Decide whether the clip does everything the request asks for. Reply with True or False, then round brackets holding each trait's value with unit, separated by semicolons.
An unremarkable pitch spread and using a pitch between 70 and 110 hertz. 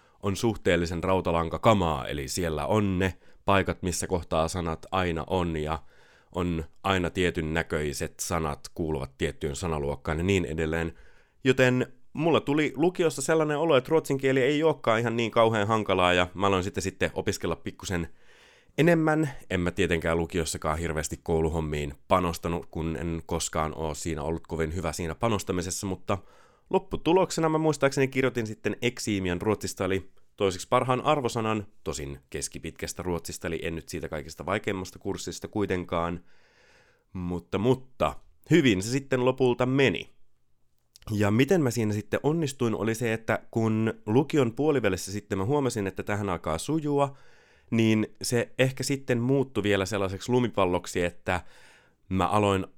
False (6.1 semitones; 95 Hz)